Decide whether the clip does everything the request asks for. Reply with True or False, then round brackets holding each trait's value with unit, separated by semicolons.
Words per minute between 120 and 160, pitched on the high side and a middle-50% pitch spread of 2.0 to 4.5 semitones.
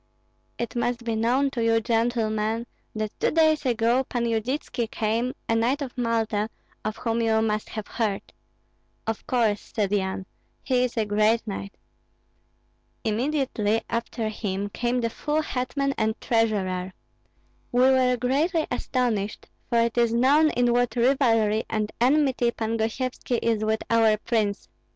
True (145 wpm; 230 Hz; 2.5 semitones)